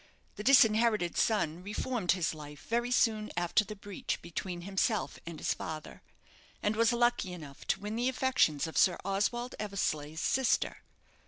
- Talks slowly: No, average, 155 wpm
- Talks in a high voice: Yes, high, 205 Hz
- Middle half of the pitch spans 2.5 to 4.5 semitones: No, average, 5.2 semitones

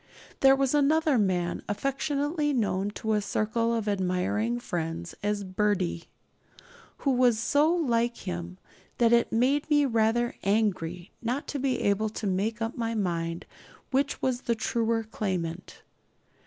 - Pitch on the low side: No, high, 225 Hz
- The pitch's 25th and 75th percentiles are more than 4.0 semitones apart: Yes, average, 4.8 semitones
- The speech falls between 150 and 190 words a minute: No, average, 140 wpm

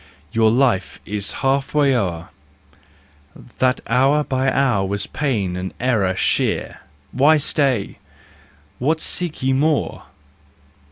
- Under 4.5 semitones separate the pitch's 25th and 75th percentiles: No, wide, 5.4 semitones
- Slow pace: Yes, slow, 115 wpm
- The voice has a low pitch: Yes, low, 130 Hz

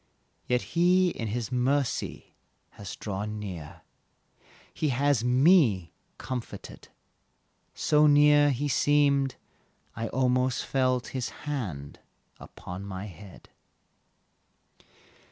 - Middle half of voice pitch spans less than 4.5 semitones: No, wide, 5.5 semitones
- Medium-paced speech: No, slow, 90 wpm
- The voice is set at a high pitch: No, low, 125 Hz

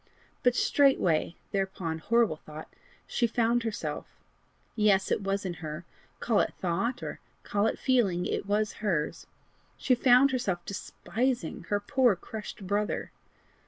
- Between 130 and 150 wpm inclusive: Yes, slow, 135 wpm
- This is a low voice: No, high, 205 Hz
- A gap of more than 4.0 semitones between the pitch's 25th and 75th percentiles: Yes, average, 5.0 semitones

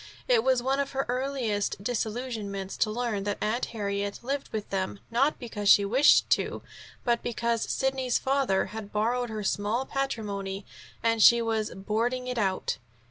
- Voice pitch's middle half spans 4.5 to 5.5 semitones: No, average, 3.6 semitones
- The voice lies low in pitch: No, high, 230 Hz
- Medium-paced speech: Yes, average, 160 wpm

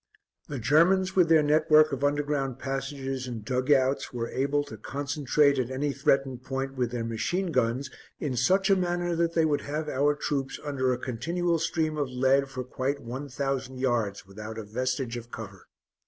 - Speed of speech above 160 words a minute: Yes, average, 185 wpm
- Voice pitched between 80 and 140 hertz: Yes, low, 135 Hz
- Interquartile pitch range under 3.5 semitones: Yes, average, 2.9 semitones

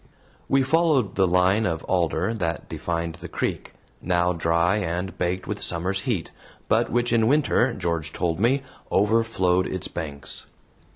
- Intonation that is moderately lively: Yes, average, 5.0 semitones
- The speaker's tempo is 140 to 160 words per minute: Yes, average, 150 wpm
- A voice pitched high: No, very low, 95 Hz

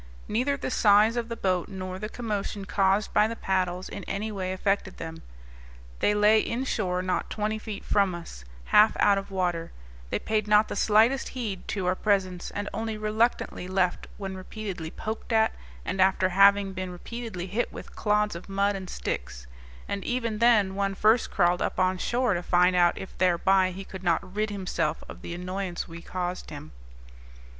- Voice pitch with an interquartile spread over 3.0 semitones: No, average, 2.7 semitones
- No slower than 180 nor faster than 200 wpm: Yes, average, 185 wpm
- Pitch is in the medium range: No, high, 195 Hz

